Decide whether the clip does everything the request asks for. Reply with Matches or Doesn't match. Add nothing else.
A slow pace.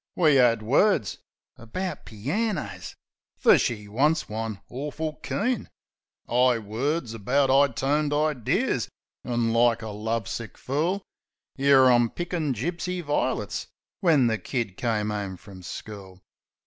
Matches